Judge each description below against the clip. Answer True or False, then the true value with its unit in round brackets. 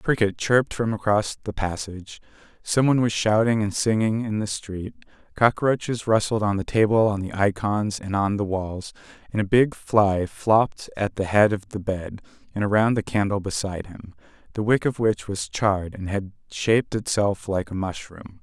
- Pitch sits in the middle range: False (105 Hz)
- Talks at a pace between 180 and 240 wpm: True (185 wpm)